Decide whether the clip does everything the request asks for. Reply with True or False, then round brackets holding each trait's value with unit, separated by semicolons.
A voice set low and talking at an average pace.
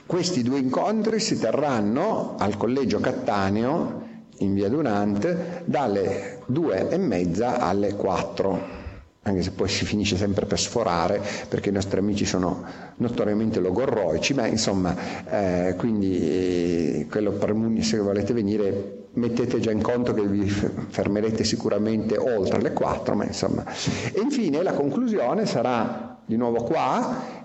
True (105 Hz; 135 wpm)